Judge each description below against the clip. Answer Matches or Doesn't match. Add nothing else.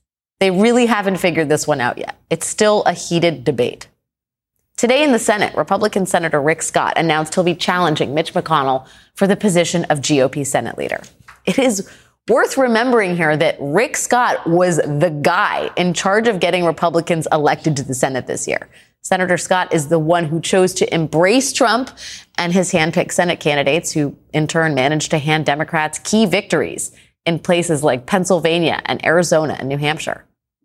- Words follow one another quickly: Doesn't match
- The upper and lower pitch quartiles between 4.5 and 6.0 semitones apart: Doesn't match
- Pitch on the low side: Doesn't match